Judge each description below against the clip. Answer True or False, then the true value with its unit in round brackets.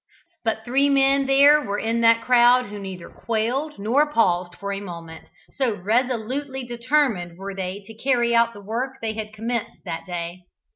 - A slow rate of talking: False (175 wpm)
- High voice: True (230 Hz)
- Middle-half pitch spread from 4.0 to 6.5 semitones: True (4.4 semitones)